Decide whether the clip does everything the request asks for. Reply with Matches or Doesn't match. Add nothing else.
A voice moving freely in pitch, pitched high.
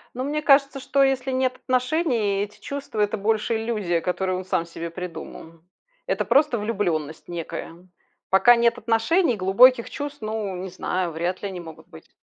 Matches